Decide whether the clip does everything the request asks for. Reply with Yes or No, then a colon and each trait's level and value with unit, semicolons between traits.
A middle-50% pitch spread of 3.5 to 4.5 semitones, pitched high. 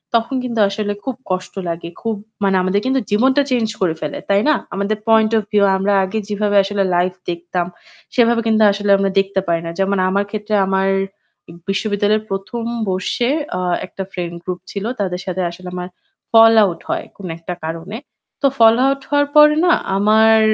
No: average, 3.1 semitones; high, 205 Hz